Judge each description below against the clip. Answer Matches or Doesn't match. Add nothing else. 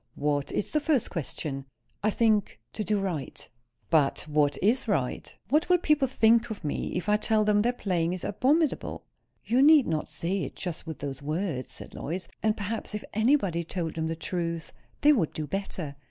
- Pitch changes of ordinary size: Doesn't match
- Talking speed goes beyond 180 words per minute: Matches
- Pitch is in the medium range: Doesn't match